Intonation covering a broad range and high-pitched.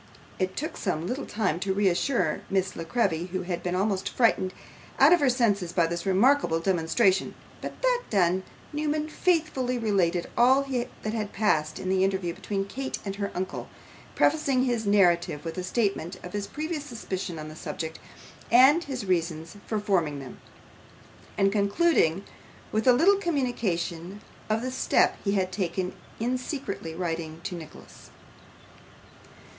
Yes: wide, 6.1 semitones; high, 195 Hz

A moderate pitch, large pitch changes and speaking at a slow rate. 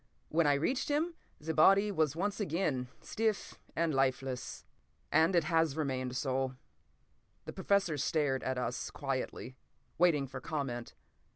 No: medium, 150 Hz; average, 4.6 semitones; slow, 130 wpm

